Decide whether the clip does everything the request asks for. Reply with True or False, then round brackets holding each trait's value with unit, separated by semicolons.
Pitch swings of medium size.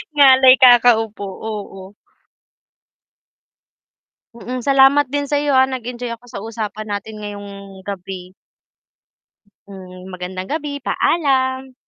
True (4.7 semitones)